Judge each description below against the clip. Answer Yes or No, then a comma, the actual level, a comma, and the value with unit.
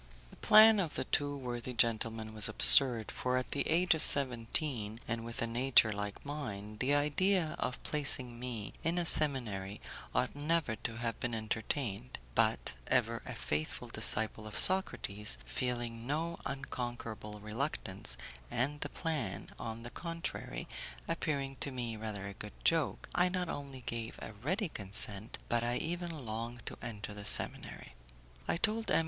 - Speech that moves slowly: No, average, 160 wpm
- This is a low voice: Yes, low, 120 Hz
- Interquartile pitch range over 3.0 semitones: Yes, average, 5.1 semitones